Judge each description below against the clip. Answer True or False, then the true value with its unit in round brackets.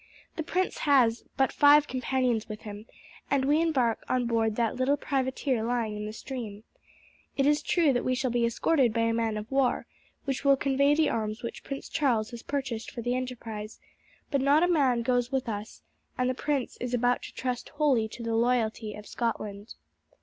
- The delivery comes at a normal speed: True (195 wpm)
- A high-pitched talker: True (245 Hz)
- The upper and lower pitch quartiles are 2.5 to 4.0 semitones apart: True (3.3 semitones)